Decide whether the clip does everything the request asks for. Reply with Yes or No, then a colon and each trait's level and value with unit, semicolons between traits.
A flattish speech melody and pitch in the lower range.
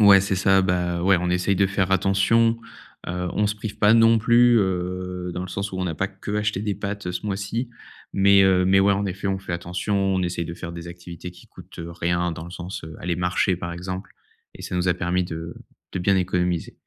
Yes: narrow, 2.0 semitones; very low, 95 Hz